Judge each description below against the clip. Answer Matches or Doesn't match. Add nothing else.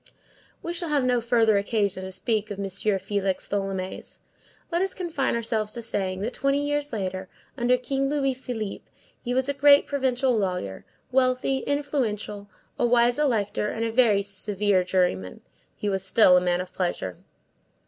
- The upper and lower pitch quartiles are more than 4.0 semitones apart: Matches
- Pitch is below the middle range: Doesn't match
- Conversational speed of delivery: Matches